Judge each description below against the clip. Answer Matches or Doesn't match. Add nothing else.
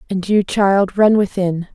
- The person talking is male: Doesn't match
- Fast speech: Doesn't match